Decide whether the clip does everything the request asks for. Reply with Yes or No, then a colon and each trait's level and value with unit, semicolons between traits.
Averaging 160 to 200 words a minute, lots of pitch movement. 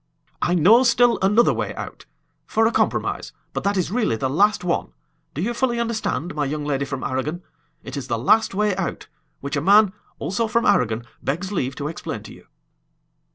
Yes: average, 195 wpm; wide, 7.7 semitones